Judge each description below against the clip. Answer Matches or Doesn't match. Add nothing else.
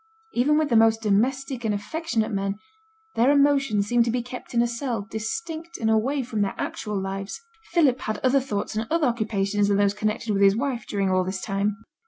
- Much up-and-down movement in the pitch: Doesn't match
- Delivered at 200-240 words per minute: Matches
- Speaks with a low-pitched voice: Doesn't match